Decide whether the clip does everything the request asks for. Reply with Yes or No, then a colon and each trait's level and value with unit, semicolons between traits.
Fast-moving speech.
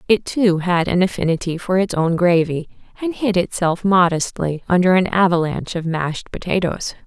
No: average, 160 wpm